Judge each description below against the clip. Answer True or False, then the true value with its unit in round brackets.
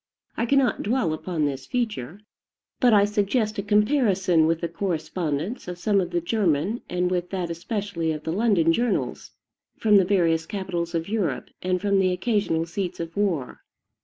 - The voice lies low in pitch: False (185 Hz)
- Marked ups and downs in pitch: False (3.9 semitones)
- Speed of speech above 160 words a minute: True (170 wpm)